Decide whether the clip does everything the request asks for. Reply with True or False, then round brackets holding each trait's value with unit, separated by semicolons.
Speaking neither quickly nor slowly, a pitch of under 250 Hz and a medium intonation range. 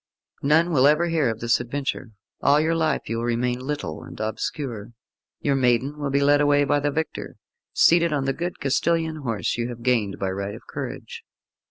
True (195 wpm; 140 Hz; 4.2 semitones)